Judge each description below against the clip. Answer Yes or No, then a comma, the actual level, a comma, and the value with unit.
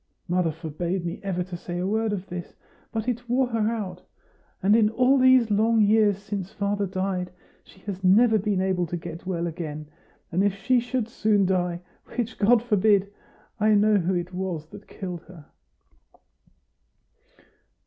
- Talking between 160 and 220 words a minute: Yes, average, 170 wpm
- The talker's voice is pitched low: No, high, 195 Hz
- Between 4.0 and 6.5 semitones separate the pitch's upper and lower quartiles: No, average, 3.4 semitones